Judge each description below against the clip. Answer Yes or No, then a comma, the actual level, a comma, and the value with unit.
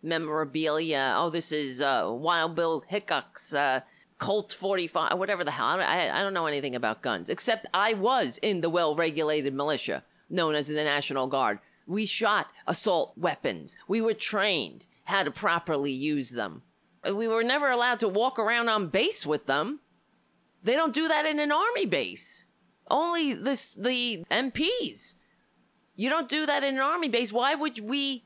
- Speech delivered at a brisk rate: No, average, 170 wpm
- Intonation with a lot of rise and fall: Yes, wide, 9.0 semitones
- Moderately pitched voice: No, high, 200 Hz